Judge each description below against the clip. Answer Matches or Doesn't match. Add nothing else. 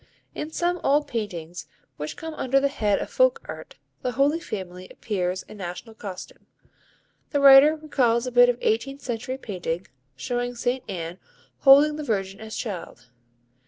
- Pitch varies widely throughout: Matches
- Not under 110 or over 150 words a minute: Doesn't match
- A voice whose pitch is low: Doesn't match